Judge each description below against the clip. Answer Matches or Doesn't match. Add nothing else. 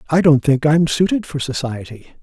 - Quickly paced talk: Doesn't match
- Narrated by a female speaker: Doesn't match